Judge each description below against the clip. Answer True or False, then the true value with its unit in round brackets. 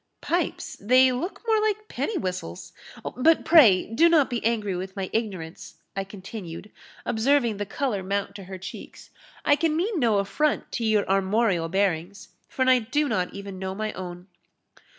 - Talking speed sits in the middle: True (170 wpm)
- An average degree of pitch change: False (6.4 semitones)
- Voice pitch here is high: True (215 Hz)